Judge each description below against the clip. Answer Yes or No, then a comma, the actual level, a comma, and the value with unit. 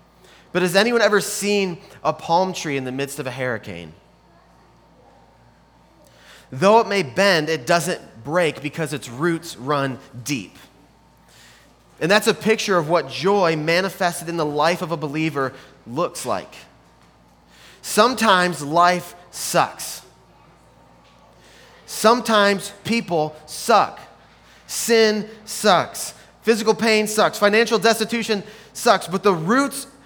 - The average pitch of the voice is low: No, medium, 175 Hz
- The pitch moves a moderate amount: No, wide, 7.0 semitones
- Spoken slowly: Yes, slow, 120 wpm